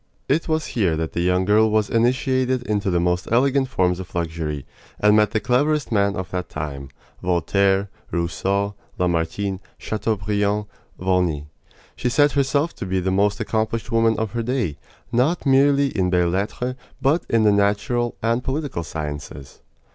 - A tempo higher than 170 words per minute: No, average, 160 wpm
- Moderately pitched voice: No, low, 105 Hz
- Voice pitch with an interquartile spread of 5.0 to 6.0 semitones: Yes, wide, 5.4 semitones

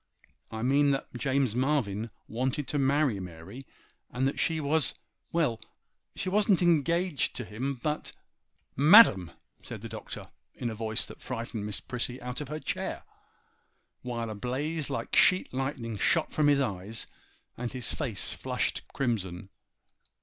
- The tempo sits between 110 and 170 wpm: Yes, average, 140 wpm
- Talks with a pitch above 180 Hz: No, low, 130 Hz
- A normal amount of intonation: Yes, average, 4.5 semitones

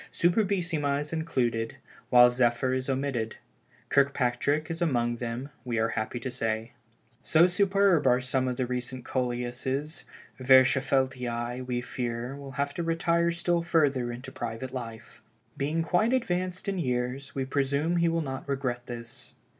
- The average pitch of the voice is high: No, low, 130 Hz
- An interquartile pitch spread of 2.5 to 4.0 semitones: No, average, 4.7 semitones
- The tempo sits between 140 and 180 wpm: Yes, average, 145 wpm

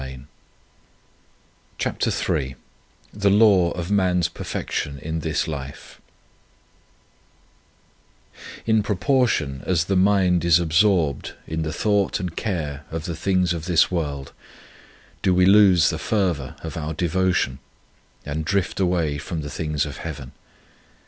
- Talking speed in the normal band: No, slow, 130 wpm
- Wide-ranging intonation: No, average, 3.6 semitones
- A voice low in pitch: Yes, very low, 85 Hz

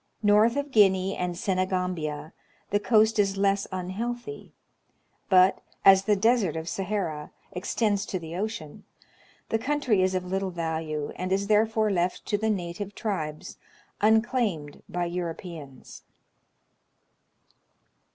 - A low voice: No, high, 190 Hz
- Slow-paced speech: Yes, slow, 125 wpm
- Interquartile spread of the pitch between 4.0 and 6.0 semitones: No, average, 3.5 semitones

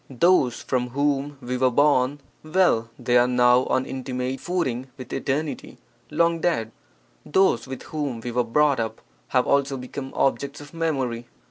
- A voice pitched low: Yes, low, 130 Hz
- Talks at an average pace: Yes, average, 155 wpm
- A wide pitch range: No, average, 3.0 semitones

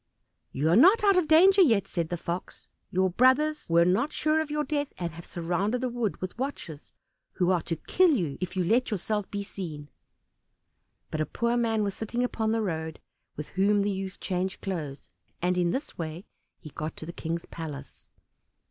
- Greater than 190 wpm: Yes, average, 200 wpm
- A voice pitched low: No, high, 195 Hz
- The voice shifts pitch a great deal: Yes, wide, 6.5 semitones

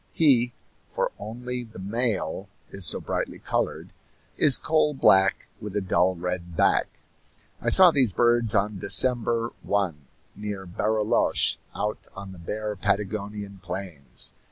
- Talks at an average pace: No, slow, 130 wpm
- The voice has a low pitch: Yes, low, 105 Hz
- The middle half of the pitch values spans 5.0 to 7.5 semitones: No, average, 3.8 semitones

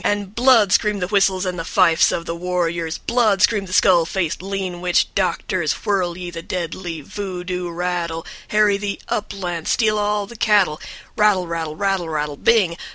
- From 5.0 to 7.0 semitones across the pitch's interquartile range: No, average, 3.1 semitones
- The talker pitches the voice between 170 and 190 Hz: Yes, medium, 185 Hz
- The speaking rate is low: No, average, 175 wpm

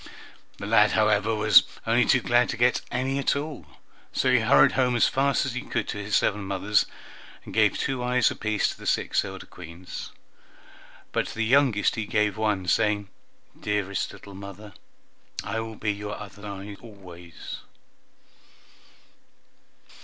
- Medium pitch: No, low, 105 Hz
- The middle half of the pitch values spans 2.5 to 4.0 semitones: Yes, average, 3.3 semitones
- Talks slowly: No, average, 160 wpm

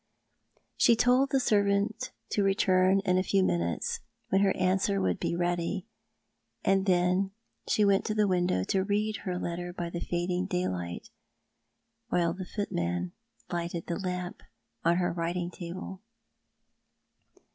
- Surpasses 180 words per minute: No, average, 140 wpm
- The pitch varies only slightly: Yes, narrow, 2.2 semitones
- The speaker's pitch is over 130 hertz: Yes, medium, 185 Hz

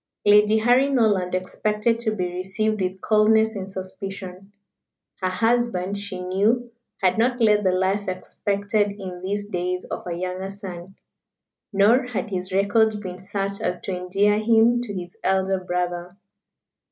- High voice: Yes, high, 200 Hz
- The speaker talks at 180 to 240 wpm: No, average, 150 wpm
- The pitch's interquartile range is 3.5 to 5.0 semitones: No, average, 2.7 semitones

